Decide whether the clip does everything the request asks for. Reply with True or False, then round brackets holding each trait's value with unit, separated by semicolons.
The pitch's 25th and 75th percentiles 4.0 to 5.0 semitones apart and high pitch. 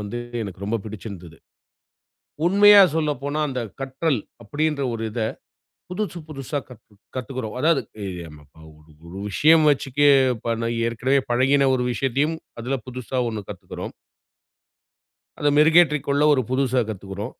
False (4.3 semitones; 130 Hz)